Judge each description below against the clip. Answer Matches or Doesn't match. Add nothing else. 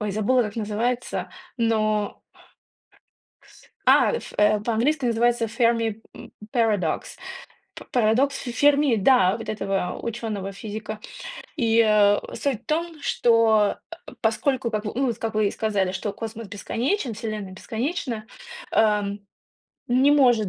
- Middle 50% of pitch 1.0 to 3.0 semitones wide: Matches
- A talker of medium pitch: Doesn't match